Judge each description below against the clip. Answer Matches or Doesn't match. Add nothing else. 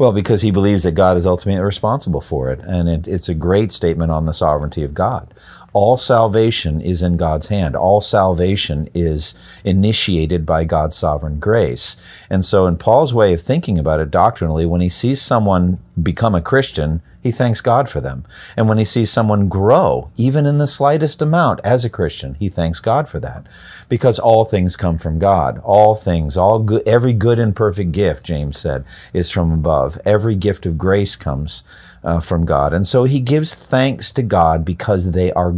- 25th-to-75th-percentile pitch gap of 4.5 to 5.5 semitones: Matches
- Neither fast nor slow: Matches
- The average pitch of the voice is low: Matches